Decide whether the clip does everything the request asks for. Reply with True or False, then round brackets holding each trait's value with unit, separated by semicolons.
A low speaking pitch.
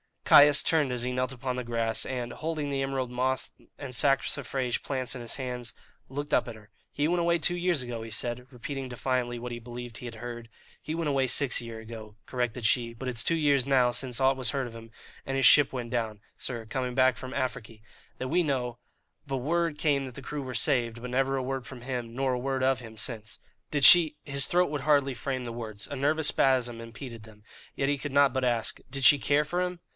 True (130 Hz)